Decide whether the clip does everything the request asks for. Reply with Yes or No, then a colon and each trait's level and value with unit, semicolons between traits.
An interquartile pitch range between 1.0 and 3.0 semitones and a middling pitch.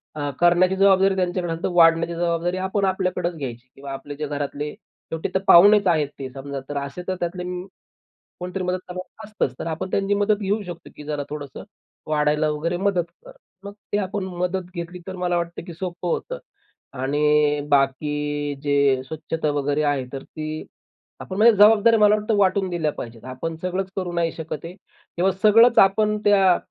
No: average, 4.4 semitones; medium, 175 Hz